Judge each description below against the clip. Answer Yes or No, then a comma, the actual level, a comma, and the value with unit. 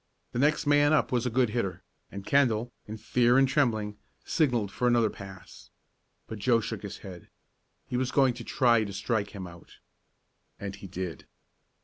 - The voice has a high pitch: No, low, 115 Hz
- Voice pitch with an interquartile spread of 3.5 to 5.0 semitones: Yes, average, 4.0 semitones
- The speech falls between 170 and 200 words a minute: Yes, average, 175 wpm